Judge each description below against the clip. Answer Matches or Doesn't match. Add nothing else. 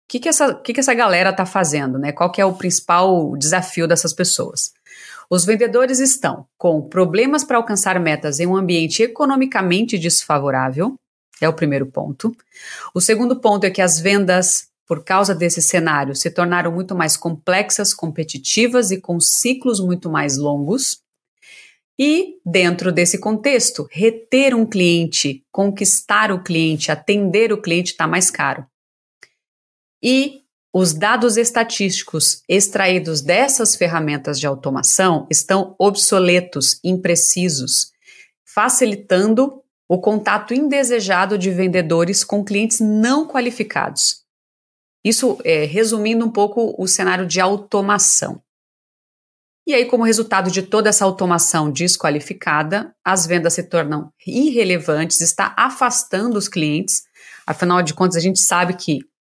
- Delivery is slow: Doesn't match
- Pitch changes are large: Doesn't match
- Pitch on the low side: Doesn't match